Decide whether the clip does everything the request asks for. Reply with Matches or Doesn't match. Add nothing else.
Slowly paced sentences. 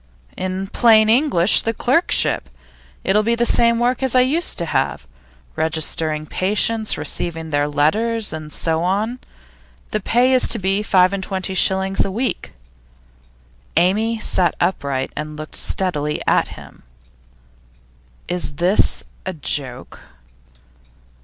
Matches